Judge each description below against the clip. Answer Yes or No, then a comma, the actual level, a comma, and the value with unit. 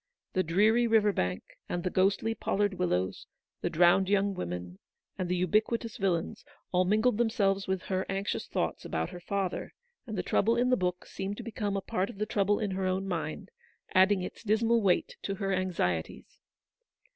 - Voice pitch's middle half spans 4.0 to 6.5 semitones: No, narrow, 2.5 semitones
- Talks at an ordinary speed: Yes, average, 190 wpm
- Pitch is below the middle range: No, high, 195 Hz